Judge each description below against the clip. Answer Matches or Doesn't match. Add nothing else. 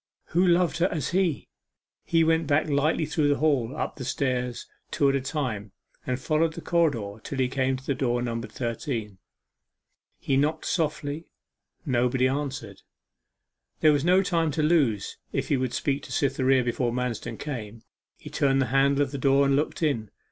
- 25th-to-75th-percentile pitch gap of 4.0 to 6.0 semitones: Doesn't match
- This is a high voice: Doesn't match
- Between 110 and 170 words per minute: Doesn't match